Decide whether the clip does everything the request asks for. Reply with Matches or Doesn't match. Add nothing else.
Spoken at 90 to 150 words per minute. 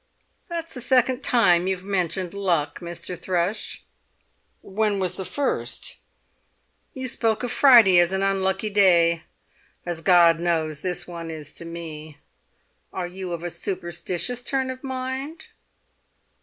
Matches